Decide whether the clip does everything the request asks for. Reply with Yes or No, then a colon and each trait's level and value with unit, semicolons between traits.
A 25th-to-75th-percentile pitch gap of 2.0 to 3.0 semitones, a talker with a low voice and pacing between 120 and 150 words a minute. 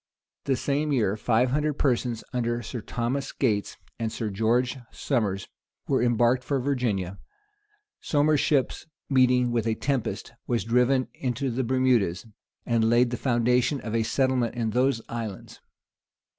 Yes: narrow, 2.4 semitones; low, 120 Hz; average, 145 wpm